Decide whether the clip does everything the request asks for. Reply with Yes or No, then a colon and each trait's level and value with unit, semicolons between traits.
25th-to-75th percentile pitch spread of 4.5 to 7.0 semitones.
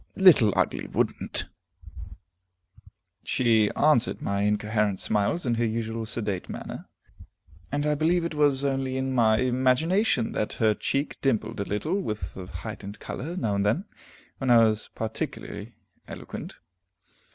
Yes: average, 4.9 semitones